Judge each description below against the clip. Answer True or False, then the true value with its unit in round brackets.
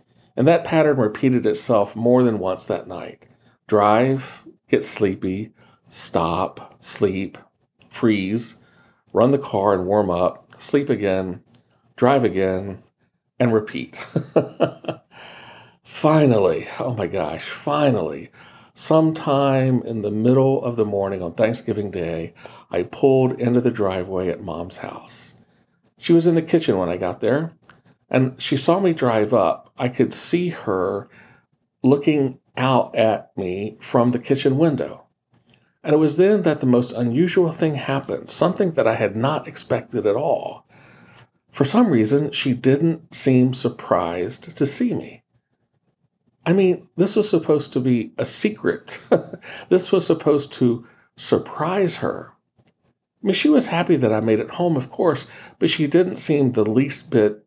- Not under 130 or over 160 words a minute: True (145 wpm)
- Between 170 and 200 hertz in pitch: False (130 Hz)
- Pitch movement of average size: False (6.0 semitones)